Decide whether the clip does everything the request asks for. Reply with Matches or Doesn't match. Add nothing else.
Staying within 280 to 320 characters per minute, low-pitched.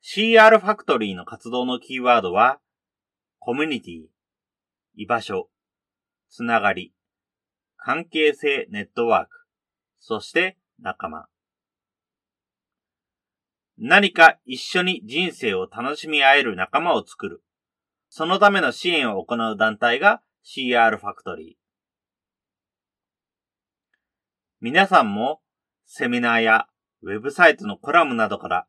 Doesn't match